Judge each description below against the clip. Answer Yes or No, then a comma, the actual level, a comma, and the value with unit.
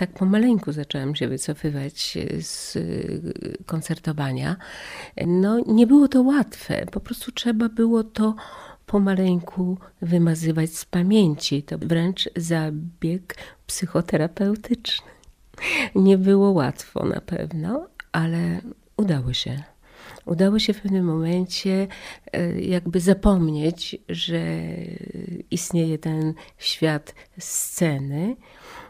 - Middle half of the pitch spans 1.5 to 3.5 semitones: No, average, 4.2 semitones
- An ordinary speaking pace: No, slow, 95 wpm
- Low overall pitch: No, medium, 180 Hz